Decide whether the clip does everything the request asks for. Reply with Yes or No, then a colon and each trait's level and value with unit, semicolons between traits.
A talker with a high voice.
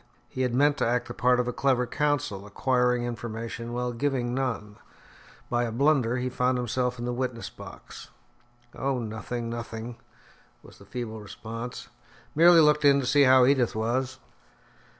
No: low, 125 Hz